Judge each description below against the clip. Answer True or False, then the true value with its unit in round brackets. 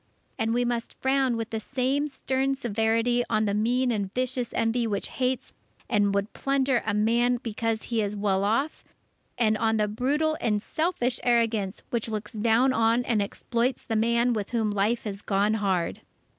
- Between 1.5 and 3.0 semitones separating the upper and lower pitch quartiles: True (2.7 semitones)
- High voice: True (230 Hz)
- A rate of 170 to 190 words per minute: True (175 wpm)